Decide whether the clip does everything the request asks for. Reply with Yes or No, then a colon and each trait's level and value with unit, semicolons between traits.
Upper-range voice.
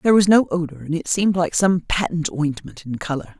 No: medium, 170 Hz